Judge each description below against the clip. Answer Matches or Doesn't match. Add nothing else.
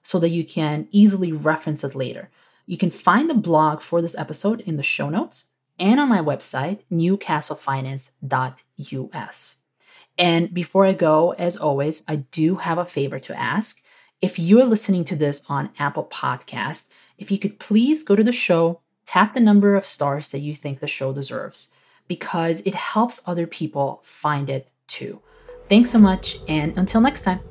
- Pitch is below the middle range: Doesn't match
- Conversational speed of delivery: Matches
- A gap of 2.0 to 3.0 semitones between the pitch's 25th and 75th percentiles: Doesn't match